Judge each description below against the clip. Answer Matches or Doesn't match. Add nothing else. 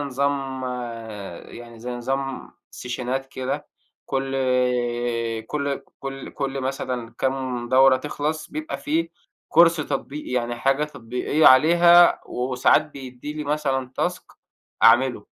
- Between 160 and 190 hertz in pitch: Doesn't match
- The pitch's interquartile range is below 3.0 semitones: Matches